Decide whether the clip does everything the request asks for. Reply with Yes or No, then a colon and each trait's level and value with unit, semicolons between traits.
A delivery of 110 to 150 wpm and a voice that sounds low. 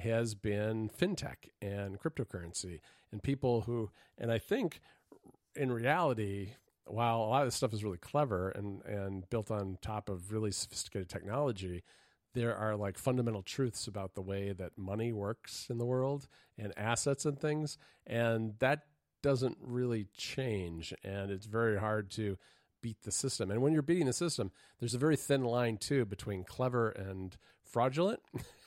No: average, 165 wpm; low, 110 Hz